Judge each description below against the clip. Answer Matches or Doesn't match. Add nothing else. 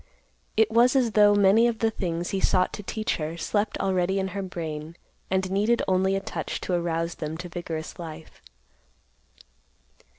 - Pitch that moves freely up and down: Doesn't match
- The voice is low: Doesn't match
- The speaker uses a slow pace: Doesn't match